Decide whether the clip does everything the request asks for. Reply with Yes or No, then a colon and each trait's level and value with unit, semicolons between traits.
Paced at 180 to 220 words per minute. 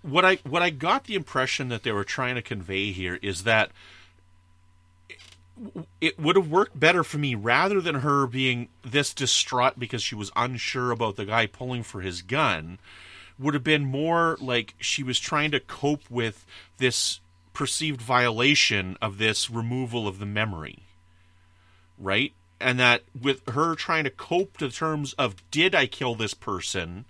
No: average, 170 wpm